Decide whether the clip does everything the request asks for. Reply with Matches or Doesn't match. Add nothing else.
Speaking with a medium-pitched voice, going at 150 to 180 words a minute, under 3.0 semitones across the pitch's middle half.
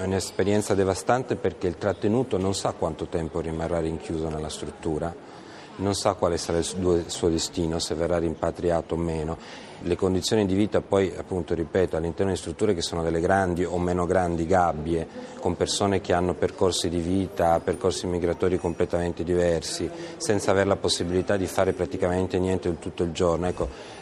Doesn't match